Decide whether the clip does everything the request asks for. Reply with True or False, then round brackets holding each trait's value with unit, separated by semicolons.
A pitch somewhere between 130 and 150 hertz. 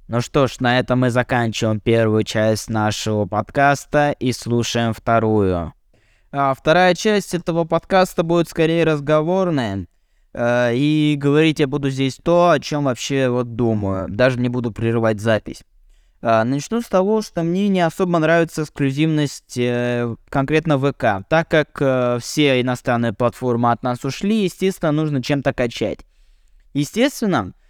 True (135 Hz)